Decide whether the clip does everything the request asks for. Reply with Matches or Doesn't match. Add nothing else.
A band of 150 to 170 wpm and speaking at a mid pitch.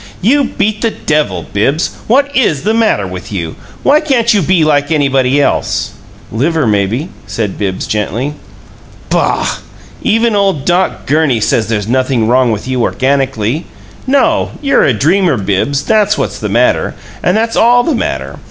Matches